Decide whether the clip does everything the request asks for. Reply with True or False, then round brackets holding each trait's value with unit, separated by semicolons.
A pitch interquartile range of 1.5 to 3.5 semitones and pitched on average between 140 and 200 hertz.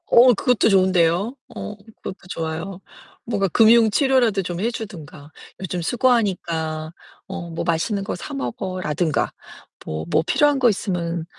False (5.2 semitones; 185 Hz)